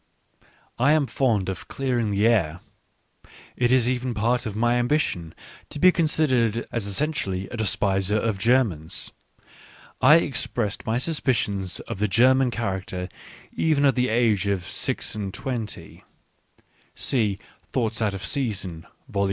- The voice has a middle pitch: No, low, 115 Hz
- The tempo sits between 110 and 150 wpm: Yes, average, 140 wpm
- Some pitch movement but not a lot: Yes, average, 4.5 semitones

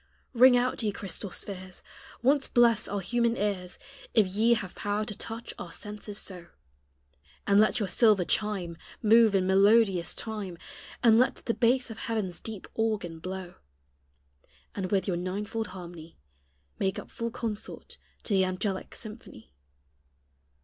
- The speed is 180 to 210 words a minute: No, average, 145 wpm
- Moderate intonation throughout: Yes, average, 3.4 semitones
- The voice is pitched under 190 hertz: No, high, 205 Hz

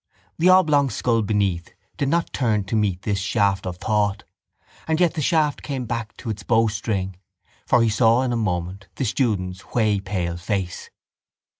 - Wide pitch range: No, average, 4.2 semitones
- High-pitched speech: No, low, 105 Hz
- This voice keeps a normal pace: Yes, average, 170 wpm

